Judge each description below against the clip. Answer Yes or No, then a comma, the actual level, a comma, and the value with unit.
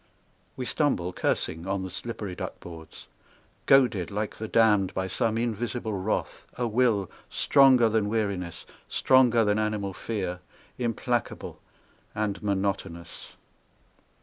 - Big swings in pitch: No, average, 3.6 semitones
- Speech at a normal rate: No, slow, 120 wpm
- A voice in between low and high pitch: No, low, 105 Hz